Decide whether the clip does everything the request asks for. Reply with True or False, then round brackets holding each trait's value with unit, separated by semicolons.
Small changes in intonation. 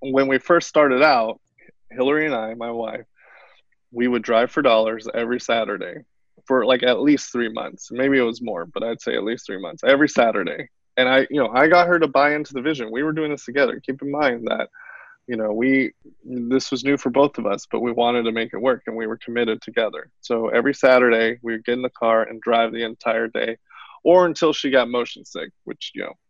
False (3.3 semitones)